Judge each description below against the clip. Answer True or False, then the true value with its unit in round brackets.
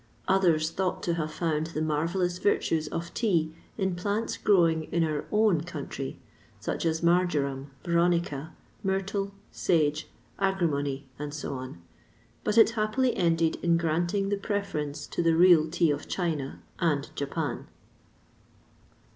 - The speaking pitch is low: False (170 Hz)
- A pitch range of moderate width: True (3.6 semitones)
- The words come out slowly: True (130 wpm)